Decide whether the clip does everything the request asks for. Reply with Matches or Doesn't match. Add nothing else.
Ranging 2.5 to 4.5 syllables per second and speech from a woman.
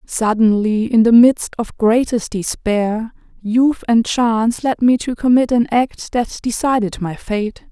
Matches